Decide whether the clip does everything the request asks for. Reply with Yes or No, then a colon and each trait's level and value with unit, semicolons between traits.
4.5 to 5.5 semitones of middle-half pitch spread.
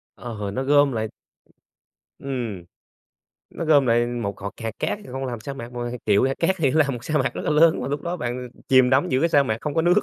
No: average, 3.8 semitones